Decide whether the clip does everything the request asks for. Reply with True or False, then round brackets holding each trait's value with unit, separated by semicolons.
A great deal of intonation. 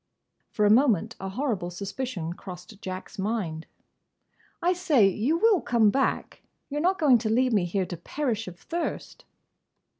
True (6.5 semitones)